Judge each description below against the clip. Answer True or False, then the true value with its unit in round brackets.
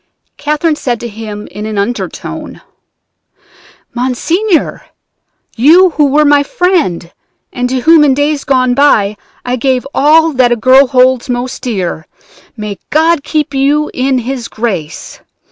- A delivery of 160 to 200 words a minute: False (140 wpm)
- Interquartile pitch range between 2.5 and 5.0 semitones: True (3.9 semitones)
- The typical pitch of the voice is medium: False (260 Hz)